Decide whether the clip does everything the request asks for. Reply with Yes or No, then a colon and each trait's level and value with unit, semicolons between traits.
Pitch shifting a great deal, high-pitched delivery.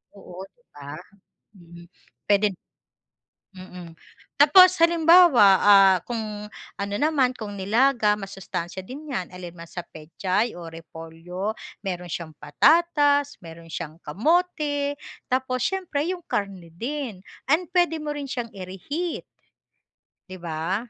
Yes: wide, 8.5 semitones; high, 205 Hz